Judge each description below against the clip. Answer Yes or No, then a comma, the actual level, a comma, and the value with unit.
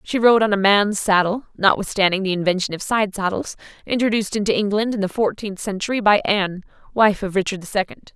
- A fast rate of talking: No, average, 190 wpm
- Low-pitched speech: No, high, 200 Hz